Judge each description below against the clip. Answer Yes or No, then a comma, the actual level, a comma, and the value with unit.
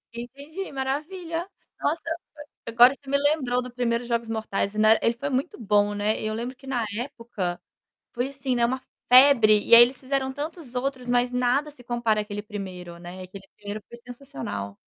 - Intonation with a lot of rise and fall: No, average, 4.0 semitones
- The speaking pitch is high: Yes, high, 245 Hz